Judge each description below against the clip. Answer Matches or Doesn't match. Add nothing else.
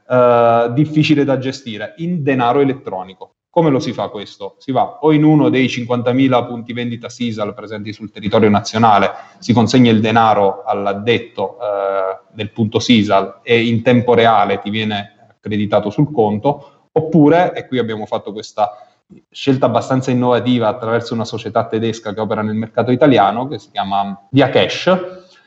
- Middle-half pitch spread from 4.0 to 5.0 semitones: Doesn't match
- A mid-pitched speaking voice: Doesn't match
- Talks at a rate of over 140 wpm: Matches